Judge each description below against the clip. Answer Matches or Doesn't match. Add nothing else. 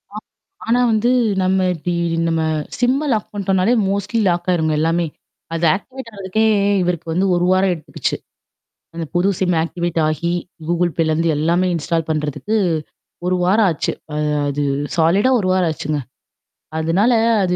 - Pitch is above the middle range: Doesn't match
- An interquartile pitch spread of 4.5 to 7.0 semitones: Doesn't match